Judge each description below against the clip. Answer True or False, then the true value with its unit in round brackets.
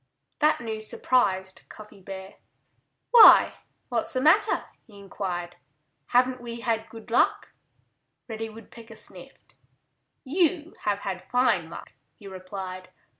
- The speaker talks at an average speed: False (120 wpm)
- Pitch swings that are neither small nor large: True (4.4 semitones)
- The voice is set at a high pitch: True (225 Hz)